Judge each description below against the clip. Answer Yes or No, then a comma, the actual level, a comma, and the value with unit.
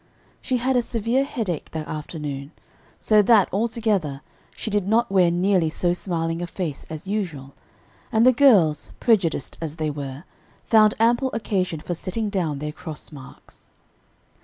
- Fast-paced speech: No, average, 155 wpm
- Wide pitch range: Yes, wide, 5.9 semitones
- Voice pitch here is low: No, medium, 185 Hz